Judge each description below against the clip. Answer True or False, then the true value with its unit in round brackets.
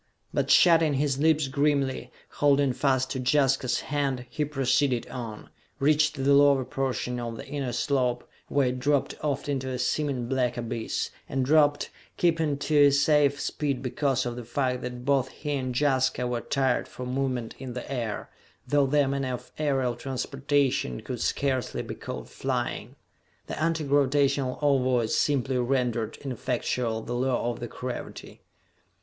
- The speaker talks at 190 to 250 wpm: False (155 wpm)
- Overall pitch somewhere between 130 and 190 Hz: True (135 Hz)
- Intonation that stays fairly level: True (2.3 semitones)